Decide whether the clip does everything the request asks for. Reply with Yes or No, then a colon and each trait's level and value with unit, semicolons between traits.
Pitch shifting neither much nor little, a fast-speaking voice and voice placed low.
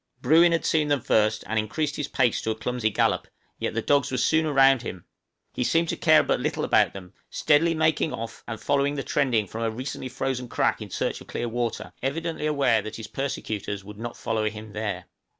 Yes: average, 4.8 semitones; fast, 215 wpm; low, 125 Hz